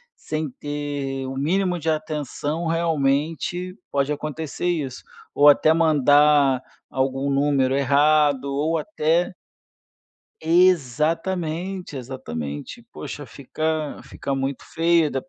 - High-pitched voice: No, medium, 150 Hz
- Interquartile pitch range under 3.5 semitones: Yes, average, 2.9 semitones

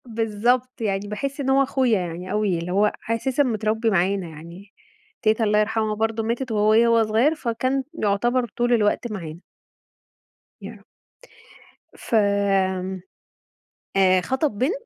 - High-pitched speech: Yes, high, 220 Hz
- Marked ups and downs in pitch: No, average, 3.4 semitones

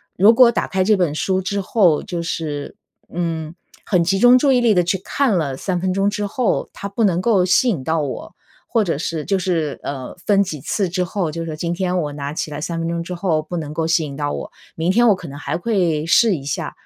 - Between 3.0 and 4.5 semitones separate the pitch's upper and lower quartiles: Yes, average, 4.0 semitones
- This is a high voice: No, medium, 175 Hz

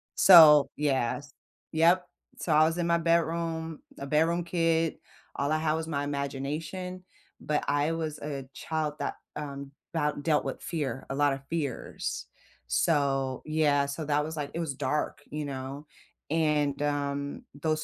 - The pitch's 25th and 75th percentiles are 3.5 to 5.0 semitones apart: No, narrow, 2.4 semitones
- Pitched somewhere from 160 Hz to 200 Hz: No, medium, 150 Hz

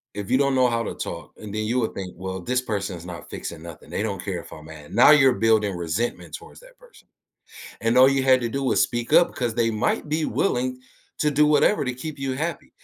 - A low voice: Yes, low, 120 Hz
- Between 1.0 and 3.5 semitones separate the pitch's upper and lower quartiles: No, average, 5.3 semitones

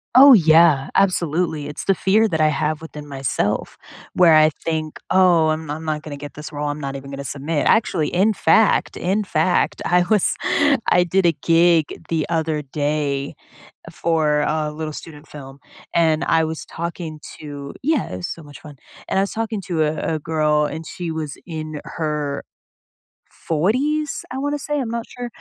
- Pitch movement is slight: No, average, 3.1 semitones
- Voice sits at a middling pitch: Yes, medium, 160 Hz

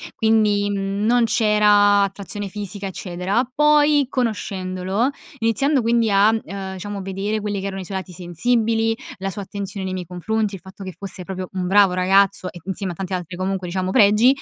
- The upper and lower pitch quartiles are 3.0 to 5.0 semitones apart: No, narrow, 2.6 semitones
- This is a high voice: Yes, high, 200 Hz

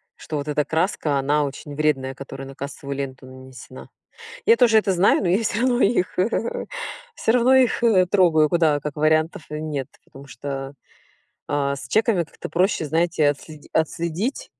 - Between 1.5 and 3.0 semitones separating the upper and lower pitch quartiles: No, average, 4.5 semitones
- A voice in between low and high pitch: Yes, medium, 155 Hz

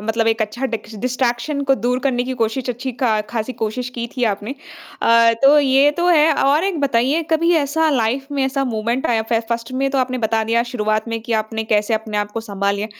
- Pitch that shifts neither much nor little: Yes, average, 3.5 semitones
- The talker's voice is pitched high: Yes, high, 240 Hz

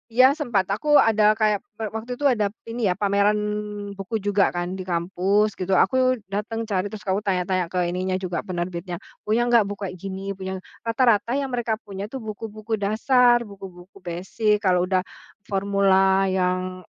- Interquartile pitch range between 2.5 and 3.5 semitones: Yes, average, 2.9 semitones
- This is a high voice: Yes, high, 200 Hz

